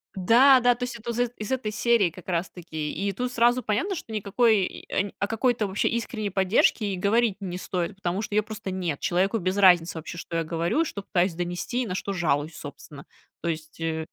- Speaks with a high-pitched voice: Yes, high, 195 Hz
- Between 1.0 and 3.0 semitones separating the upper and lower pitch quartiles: No, average, 4.7 semitones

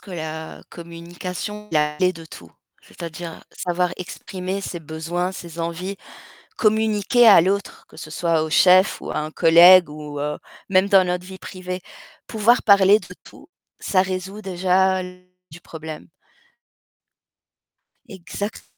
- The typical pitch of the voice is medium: Yes, medium, 180 Hz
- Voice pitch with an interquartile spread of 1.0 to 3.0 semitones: Yes, narrow, 2.6 semitones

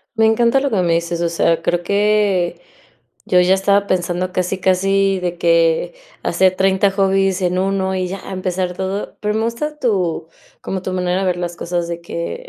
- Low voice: No, medium, 185 Hz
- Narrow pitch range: Yes, narrow, 2.0 semitones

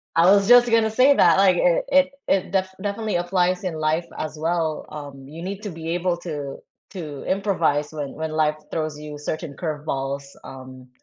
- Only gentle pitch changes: No, average, 4.1 semitones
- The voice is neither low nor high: Yes, medium, 165 Hz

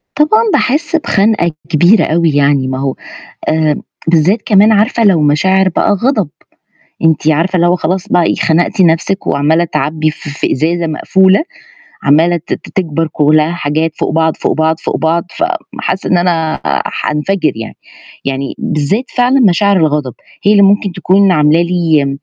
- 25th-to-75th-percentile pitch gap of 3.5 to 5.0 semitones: Yes, average, 4.1 semitones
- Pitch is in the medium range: Yes, medium, 170 Hz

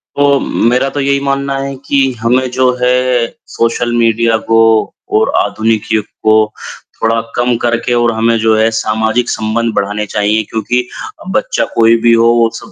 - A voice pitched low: Yes, low, 115 Hz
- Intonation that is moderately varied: No, narrow, 2.1 semitones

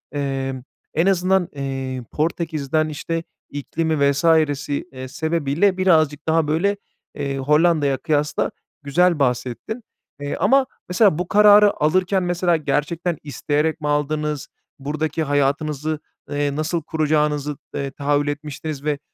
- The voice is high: No, medium, 150 Hz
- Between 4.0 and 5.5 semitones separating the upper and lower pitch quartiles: No, average, 2.9 semitones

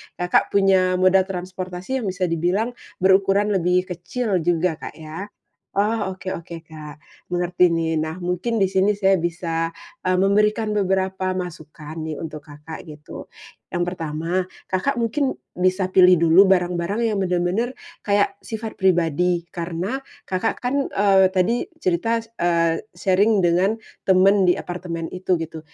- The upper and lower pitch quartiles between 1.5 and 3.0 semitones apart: Yes, average, 2.7 semitones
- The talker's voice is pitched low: No, medium, 185 Hz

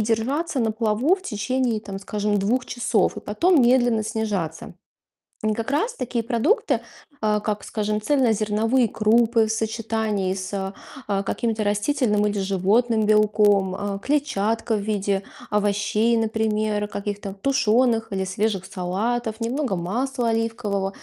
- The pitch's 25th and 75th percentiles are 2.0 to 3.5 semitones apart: Yes, narrow, 2.5 semitones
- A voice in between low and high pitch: No, high, 215 Hz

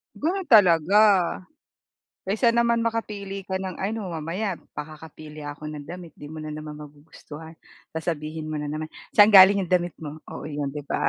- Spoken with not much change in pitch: No, average, 4.7 semitones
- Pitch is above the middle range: No, medium, 165 Hz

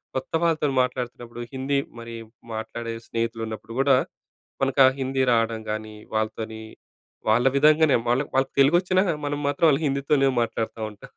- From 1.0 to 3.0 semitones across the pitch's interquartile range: No, average, 3.5 semitones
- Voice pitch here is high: No, low, 130 Hz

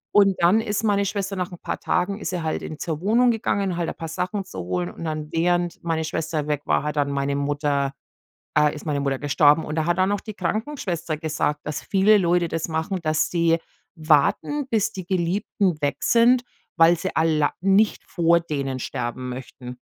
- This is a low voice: No, medium, 165 Hz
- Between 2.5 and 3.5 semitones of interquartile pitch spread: No, average, 4.6 semitones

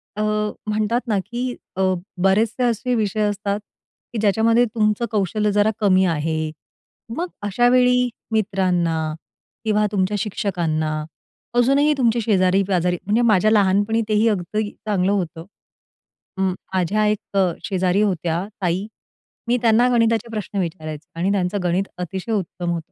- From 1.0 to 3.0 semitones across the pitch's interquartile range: No, average, 3.4 semitones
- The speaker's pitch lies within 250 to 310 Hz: No, high, 205 Hz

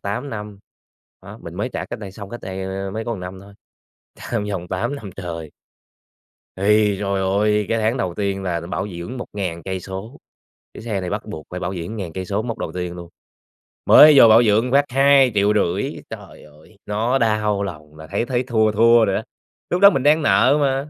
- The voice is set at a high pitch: No, low, 105 Hz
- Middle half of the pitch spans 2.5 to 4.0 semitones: Yes, average, 3.6 semitones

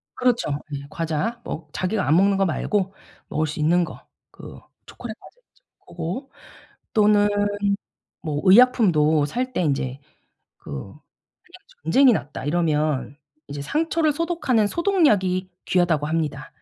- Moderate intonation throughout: No, wide, 7.6 semitones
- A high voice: No, medium, 180 Hz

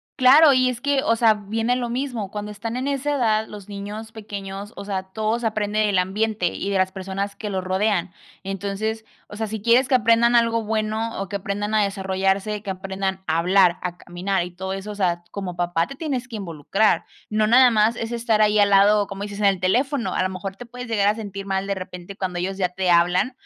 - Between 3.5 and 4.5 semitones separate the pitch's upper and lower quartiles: No, average, 2.9 semitones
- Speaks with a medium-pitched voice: No, high, 205 Hz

